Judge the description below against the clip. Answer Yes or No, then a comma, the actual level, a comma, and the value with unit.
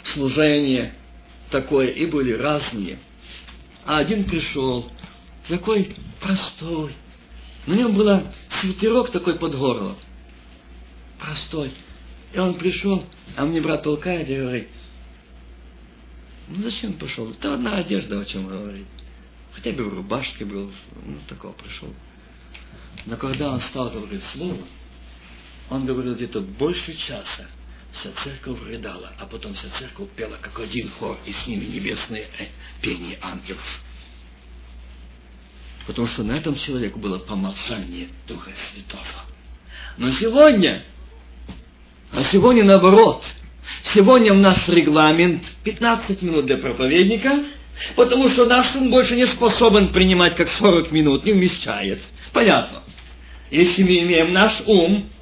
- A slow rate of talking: No, average, 125 wpm